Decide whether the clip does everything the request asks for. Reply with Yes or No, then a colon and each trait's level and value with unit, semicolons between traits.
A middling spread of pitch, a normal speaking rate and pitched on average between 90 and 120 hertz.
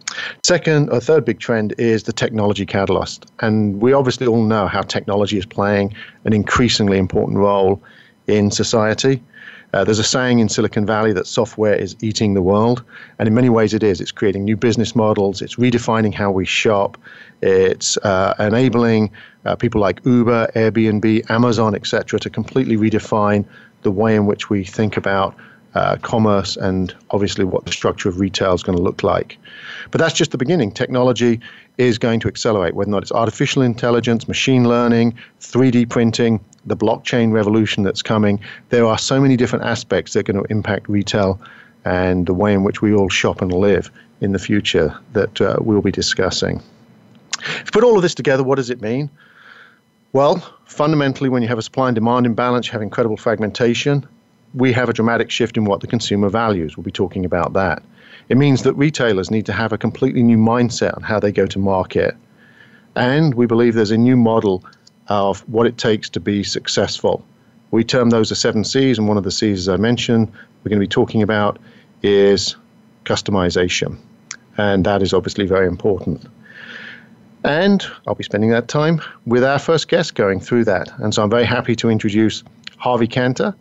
Yes: average, 3.0 semitones; average, 190 wpm; low, 110 Hz